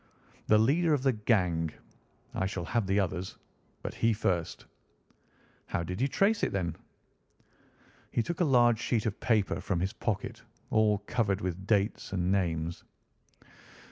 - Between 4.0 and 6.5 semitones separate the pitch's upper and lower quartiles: Yes, average, 4.3 semitones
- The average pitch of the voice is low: Yes, low, 100 Hz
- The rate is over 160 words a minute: No, average, 150 wpm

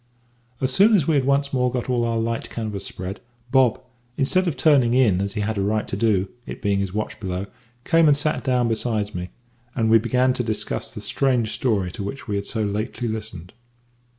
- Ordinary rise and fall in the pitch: Yes, average, 4.2 semitones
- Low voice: Yes, low, 115 Hz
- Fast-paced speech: Yes, fast, 215 wpm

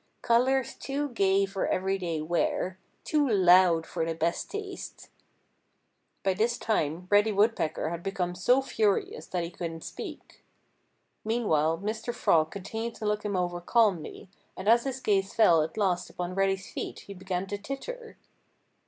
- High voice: Yes, high, 195 Hz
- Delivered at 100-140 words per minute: No, average, 155 wpm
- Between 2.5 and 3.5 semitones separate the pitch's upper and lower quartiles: No, average, 4.2 semitones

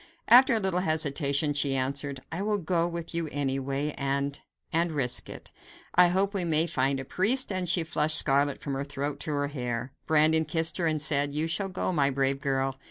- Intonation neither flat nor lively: Yes, average, 3.6 semitones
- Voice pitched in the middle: Yes, medium, 150 Hz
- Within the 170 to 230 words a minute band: Yes, fast, 205 wpm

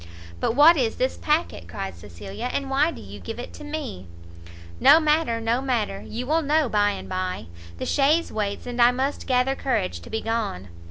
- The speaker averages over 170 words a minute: Yes, average, 200 wpm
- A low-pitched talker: No, high, 245 Hz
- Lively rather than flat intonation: Yes, wide, 6.0 semitones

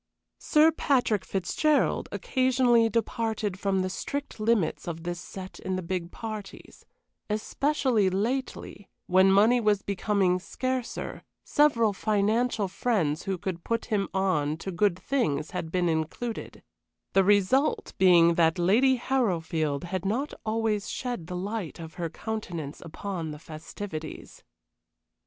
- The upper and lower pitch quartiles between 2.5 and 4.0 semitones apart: No, average, 4.8 semitones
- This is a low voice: No, high, 195 Hz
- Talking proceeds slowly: Yes, slow, 130 wpm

